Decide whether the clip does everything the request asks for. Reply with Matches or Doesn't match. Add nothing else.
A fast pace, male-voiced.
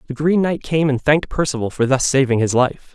Matches